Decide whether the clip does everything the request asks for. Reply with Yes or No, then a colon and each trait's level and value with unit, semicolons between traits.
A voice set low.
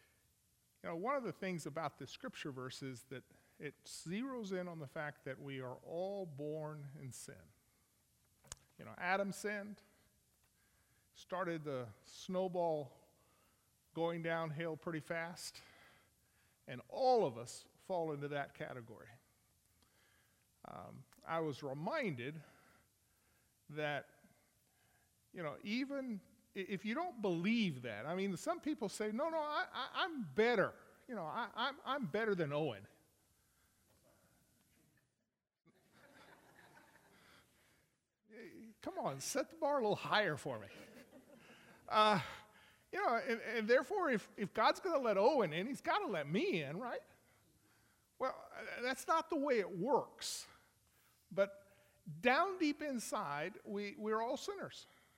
No: high, 190 Hz